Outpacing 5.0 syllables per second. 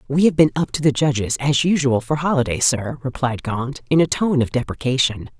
Yes: 5.4 syllables/s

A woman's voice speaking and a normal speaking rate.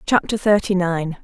Yes: female; average, 145 wpm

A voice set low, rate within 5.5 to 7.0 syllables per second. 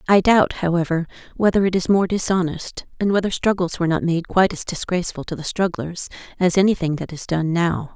No: medium, 175 Hz; 5.8 syllables/s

